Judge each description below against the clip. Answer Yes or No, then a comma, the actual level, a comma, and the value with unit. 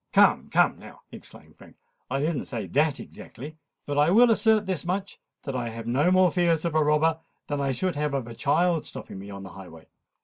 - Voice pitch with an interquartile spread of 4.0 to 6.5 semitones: Yes, wide, 5.5 semitones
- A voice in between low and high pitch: Yes, medium, 150 Hz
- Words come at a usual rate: No, fast, 210 wpm